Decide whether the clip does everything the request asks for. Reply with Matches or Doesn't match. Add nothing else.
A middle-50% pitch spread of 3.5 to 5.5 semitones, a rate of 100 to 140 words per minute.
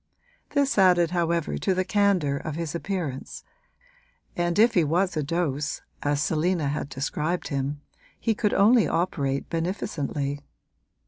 Matches